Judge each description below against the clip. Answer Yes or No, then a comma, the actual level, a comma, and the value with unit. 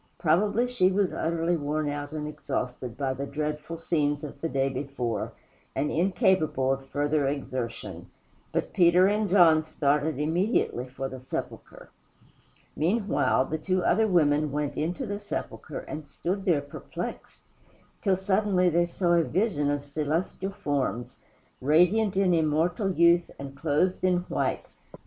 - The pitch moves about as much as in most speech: Yes, average, 4.1 semitones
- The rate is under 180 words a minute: Yes, average, 145 wpm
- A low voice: No, medium, 155 Hz